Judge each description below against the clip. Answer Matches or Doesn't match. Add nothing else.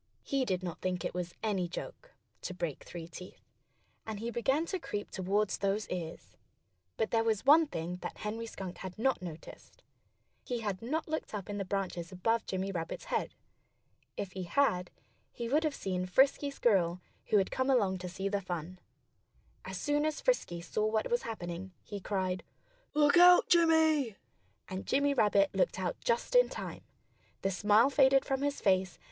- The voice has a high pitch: Matches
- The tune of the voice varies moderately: Doesn't match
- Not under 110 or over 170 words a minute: Doesn't match